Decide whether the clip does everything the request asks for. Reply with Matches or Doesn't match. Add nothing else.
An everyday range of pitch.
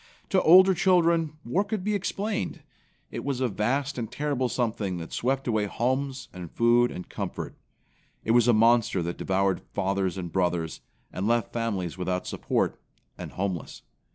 Doesn't match